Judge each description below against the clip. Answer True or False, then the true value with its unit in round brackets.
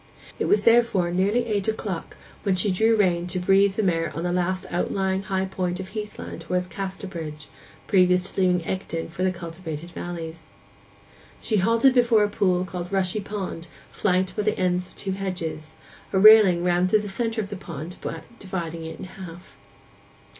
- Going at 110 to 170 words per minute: False (180 wpm)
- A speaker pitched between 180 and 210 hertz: True (185 Hz)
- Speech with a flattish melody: True (2.3 semitones)